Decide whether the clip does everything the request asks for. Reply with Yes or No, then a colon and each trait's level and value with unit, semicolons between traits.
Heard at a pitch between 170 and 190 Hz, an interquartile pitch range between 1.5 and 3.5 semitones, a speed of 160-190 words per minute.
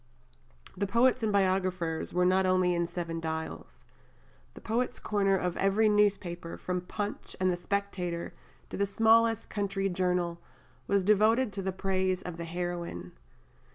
No: medium, 185 Hz; narrow, 2.5 semitones; average, 150 wpm